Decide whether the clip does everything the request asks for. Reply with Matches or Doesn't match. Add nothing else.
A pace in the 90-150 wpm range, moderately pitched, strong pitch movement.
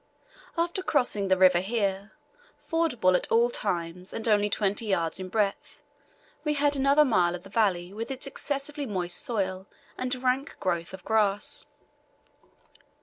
Doesn't match